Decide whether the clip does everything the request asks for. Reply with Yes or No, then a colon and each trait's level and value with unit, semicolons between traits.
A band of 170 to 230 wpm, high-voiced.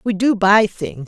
Yes: fast, 225 wpm; high, 205 Hz